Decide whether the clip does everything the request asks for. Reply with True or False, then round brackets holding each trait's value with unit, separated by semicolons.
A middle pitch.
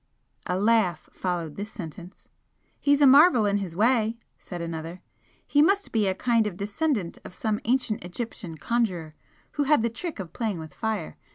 False (210 Hz)